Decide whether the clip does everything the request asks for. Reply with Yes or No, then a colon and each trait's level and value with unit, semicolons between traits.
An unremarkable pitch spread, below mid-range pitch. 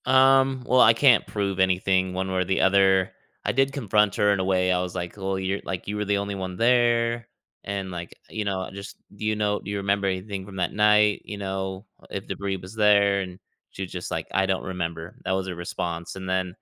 No: narrow, 2.1 semitones; very low, 95 Hz